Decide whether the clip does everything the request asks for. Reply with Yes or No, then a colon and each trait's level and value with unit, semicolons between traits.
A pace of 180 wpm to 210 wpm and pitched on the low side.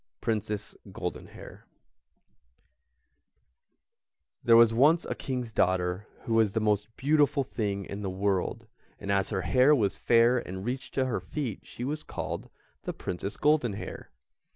No: average, 140 wpm; low, 115 Hz